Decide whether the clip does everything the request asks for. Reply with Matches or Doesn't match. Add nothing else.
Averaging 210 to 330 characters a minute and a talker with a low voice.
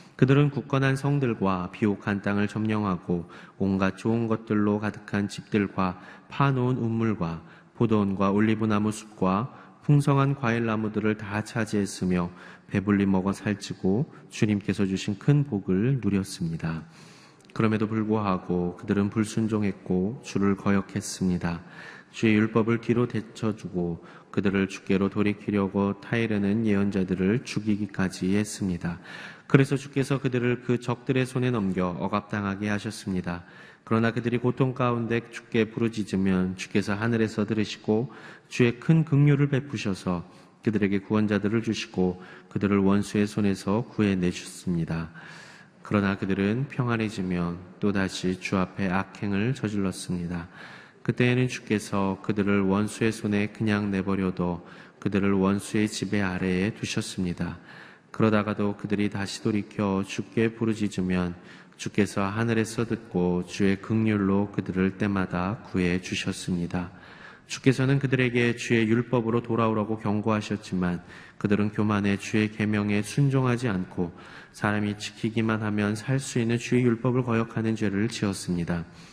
Matches